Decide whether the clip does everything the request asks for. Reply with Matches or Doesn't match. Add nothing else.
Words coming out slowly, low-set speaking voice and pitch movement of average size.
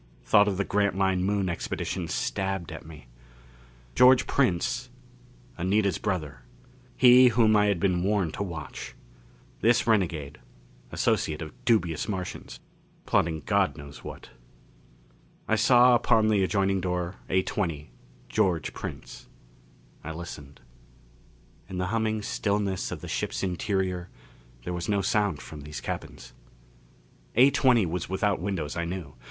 Matches